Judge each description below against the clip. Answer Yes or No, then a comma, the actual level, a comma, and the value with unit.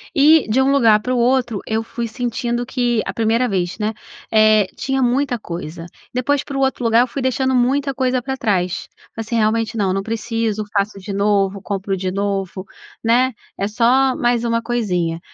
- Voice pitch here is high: Yes, high, 230 Hz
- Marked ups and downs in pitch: No, average, 3.8 semitones